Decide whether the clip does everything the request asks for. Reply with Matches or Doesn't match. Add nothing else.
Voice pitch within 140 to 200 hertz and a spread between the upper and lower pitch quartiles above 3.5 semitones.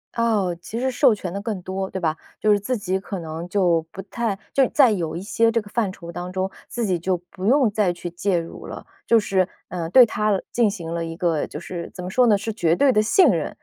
Matches